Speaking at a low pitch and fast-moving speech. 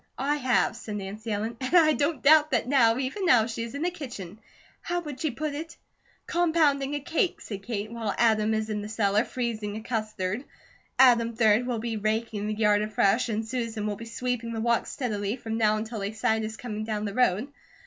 No: high, 230 Hz; fast, 210 wpm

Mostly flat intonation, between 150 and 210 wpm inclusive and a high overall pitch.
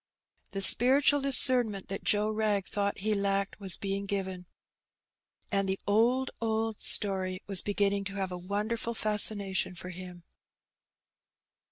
No: narrow, 2.1 semitones; slow, 135 wpm; high, 200 Hz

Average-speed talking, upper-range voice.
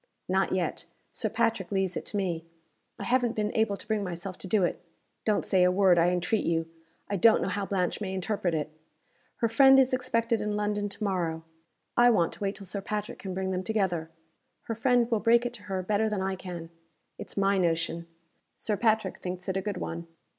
No: fast, 215 wpm; high, 200 Hz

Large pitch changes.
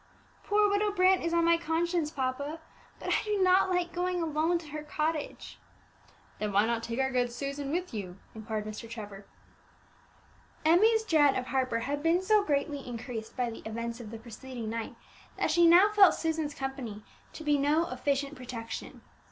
Yes: wide, 6.4 semitones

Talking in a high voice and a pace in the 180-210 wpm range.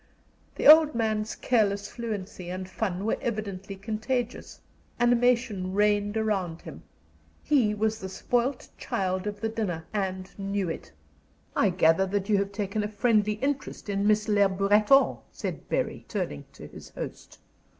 No: high, 210 Hz; average, 150 wpm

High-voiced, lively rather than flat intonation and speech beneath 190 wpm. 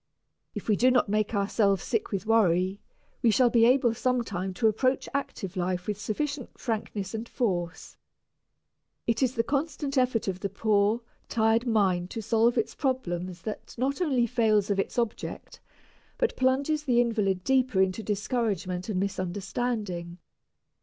No: high, 220 Hz; average, 4.3 semitones; average, 155 wpm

